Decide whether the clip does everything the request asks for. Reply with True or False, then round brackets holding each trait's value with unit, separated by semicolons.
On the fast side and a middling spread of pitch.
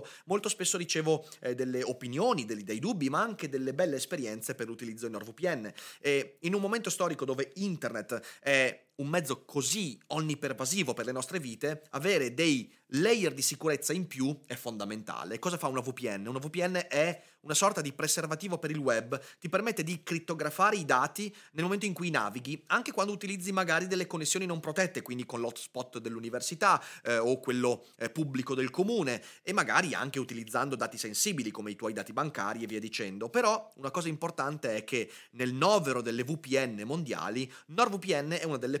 False (180 wpm; 6.0 semitones)